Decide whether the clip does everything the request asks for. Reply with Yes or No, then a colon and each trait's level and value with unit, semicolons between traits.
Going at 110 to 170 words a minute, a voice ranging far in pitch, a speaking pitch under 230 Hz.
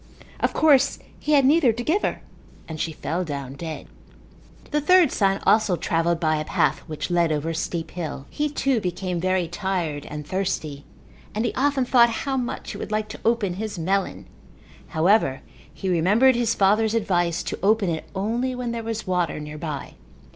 No: average, 185 wpm; wide, 6.1 semitones; high, 190 Hz